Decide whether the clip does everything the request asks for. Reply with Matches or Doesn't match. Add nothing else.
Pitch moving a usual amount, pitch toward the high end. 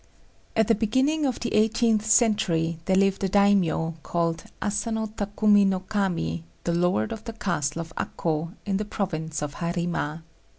Matches